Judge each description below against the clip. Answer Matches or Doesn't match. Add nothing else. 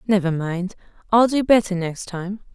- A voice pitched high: Matches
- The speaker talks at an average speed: Matches